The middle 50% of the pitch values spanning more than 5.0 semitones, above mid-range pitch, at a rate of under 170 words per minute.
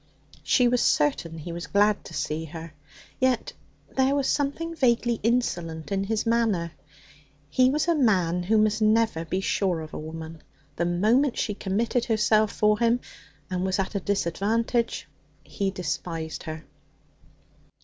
Yes: wide, 5.6 semitones; high, 205 Hz; average, 150 wpm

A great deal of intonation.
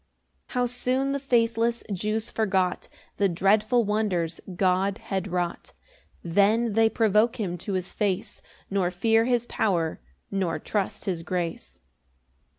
No: average, 3.7 semitones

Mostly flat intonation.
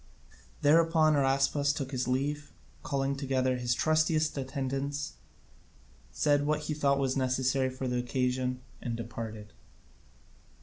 Yes: narrow, 2.3 semitones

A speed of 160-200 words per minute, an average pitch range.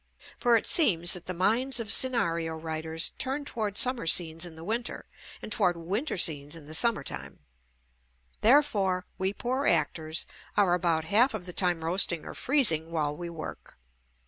No: average, 175 wpm; wide, 6.1 semitones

